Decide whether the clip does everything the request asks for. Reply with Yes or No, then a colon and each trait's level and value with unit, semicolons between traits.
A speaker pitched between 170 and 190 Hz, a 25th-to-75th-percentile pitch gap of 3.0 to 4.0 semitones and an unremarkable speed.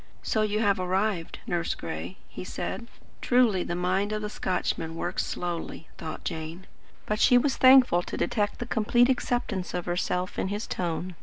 Yes: medium, 185 Hz; average, 3.7 semitones; average, 170 wpm